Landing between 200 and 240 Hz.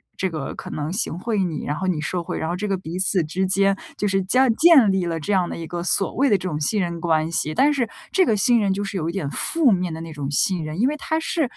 No: high, 190 Hz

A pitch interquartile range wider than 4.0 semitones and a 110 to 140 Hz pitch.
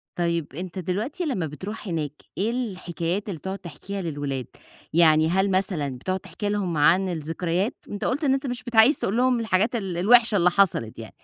No: average, 4.5 semitones; medium, 185 Hz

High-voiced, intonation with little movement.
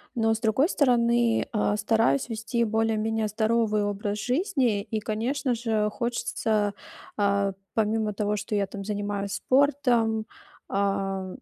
Yes: high, 220 Hz; narrow, 2.2 semitones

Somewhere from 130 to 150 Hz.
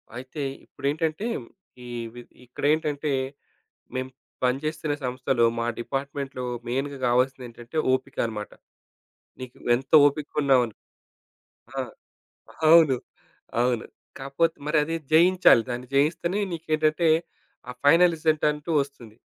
Yes: medium, 140 Hz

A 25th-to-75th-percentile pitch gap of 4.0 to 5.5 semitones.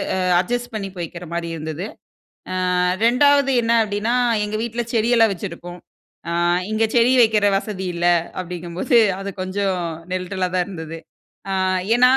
Yes: average, 4.6 semitones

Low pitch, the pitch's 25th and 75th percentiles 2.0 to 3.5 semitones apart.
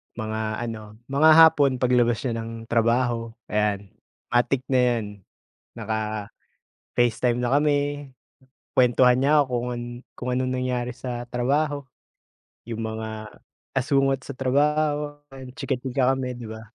Yes: low, 125 Hz; average, 3.2 semitones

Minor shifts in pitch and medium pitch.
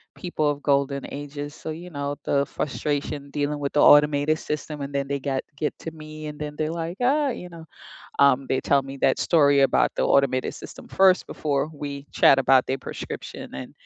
Yes: narrow, 1.7 semitones; medium, 145 Hz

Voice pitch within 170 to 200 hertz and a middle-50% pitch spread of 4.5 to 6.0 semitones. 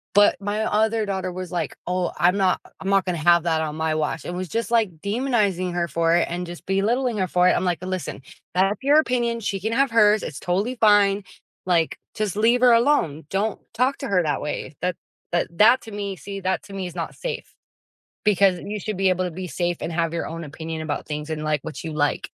No: medium, 185 Hz; average, 3.8 semitones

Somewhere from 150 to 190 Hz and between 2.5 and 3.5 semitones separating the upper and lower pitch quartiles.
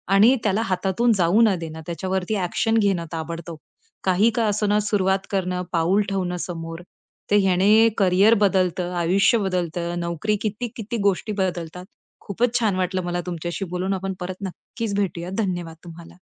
Yes: medium, 185 Hz; average, 2.8 semitones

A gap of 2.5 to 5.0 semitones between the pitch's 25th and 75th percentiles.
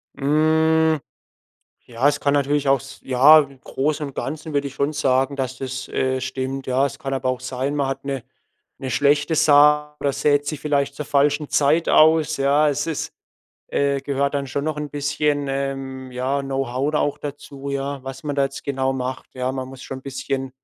No: narrow, 1.7 semitones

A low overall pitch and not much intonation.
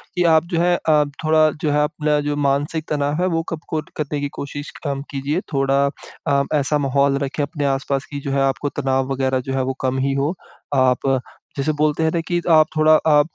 No: medium, 145 Hz; narrow, 2.1 semitones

